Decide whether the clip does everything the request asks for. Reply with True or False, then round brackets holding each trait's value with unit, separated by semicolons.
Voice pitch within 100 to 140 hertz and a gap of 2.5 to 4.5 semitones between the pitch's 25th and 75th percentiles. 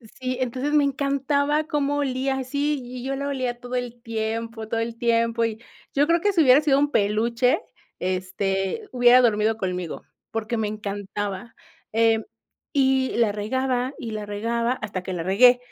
False (240 Hz; 3.6 semitones)